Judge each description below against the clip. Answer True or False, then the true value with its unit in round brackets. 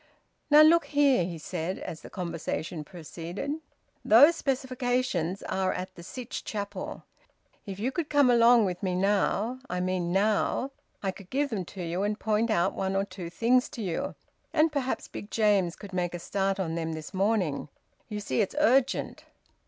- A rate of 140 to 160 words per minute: False (175 wpm)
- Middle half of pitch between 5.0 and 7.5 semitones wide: True (5.6 semitones)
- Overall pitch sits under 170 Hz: False (200 Hz)